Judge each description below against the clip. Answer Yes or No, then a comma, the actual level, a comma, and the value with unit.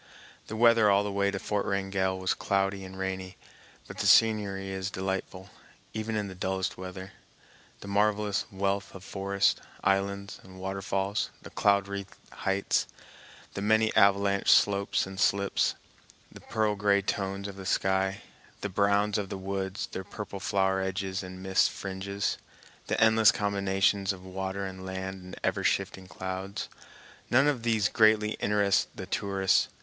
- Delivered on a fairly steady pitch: Yes, narrow, 1.1 semitones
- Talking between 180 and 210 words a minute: No, average, 155 wpm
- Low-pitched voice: Yes, low, 100 Hz